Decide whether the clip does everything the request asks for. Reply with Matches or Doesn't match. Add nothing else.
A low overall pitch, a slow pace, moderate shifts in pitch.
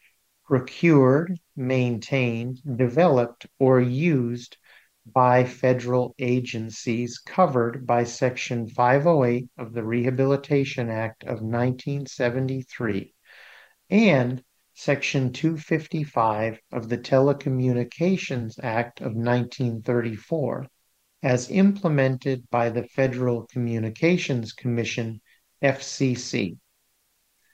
Doesn't match